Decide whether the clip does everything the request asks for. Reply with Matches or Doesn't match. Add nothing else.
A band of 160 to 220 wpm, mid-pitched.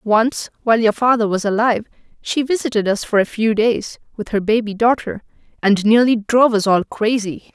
Doesn't match